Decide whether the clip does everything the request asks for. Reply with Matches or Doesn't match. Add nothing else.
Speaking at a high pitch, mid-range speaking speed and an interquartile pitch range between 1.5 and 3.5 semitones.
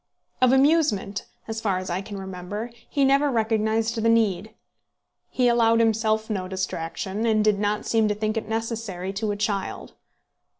Matches